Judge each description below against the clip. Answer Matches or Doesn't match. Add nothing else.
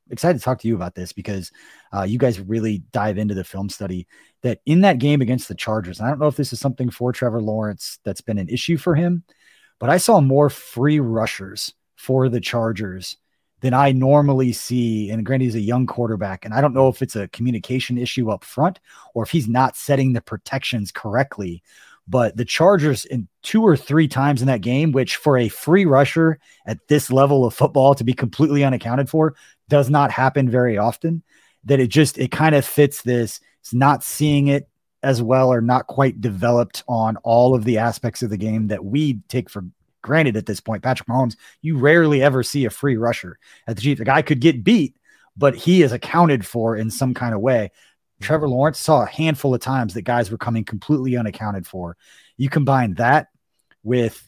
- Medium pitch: Doesn't match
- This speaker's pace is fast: Matches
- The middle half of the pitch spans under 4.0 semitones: Doesn't match